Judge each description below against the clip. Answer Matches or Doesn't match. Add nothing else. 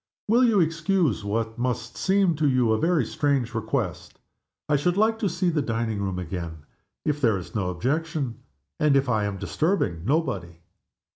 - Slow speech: Doesn't match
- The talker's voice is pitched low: Matches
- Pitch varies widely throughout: Matches